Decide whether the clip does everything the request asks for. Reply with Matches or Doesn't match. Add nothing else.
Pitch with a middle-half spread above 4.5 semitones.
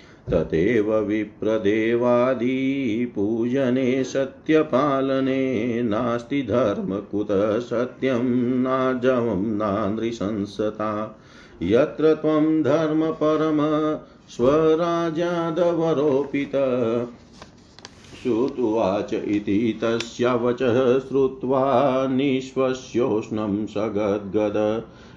Doesn't match